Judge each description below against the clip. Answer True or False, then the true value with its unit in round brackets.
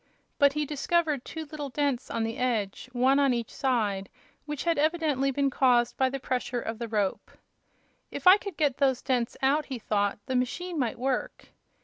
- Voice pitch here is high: True (265 Hz)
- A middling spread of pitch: True (3.5 semitones)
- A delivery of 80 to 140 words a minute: False (190 wpm)